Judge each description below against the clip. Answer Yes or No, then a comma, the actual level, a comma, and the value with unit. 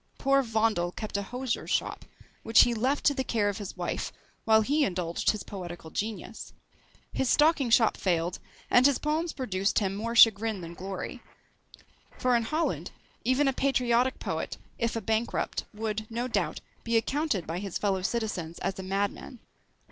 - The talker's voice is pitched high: Yes, high, 225 Hz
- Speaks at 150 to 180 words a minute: Yes, average, 170 wpm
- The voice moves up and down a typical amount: Yes, average, 4.5 semitones